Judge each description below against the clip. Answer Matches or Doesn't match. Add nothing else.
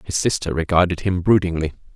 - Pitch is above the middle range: Doesn't match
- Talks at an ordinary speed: Matches